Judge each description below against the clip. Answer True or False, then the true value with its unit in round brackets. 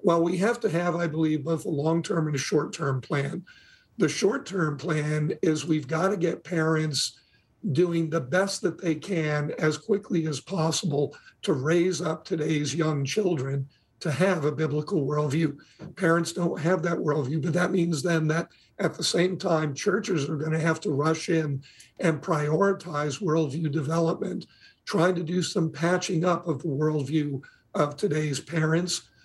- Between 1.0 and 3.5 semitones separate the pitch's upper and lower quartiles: True (2.5 semitones)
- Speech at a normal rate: True (175 wpm)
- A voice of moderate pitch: True (160 Hz)